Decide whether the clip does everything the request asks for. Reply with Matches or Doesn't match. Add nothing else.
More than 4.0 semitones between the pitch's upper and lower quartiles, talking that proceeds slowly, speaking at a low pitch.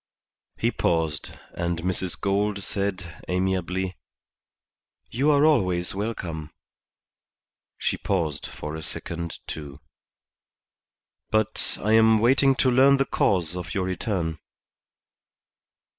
Matches